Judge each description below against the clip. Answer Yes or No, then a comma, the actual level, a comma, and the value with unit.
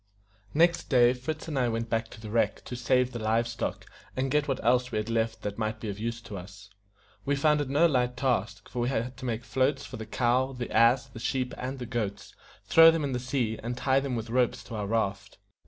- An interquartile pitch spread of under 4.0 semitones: Yes, average, 2.8 semitones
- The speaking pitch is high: No, low, 120 Hz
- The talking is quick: Yes, fast, 245 wpm